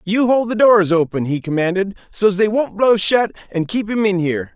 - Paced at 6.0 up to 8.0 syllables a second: No, 5.1 syllables/s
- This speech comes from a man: Yes, male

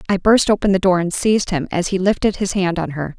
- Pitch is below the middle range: No, medium, 185 Hz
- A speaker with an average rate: No, fast, 280 wpm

